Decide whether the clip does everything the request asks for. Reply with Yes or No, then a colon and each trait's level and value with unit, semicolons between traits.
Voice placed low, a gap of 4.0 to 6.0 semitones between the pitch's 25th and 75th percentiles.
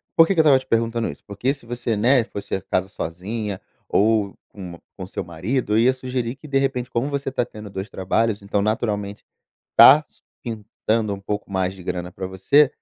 Yes: low, 110 Hz; average, 4.3 semitones